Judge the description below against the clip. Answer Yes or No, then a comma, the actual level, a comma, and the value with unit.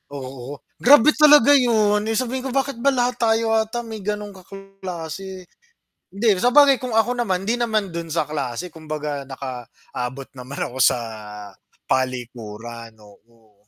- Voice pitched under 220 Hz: Yes, high, 190 Hz